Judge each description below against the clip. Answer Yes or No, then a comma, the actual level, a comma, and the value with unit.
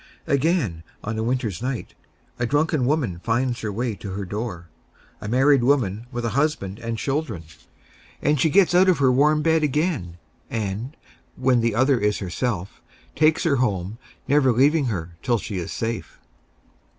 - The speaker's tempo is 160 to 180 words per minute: Yes, average, 165 wpm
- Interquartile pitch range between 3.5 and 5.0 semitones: No, wide, 5.6 semitones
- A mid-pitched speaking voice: No, low, 120 Hz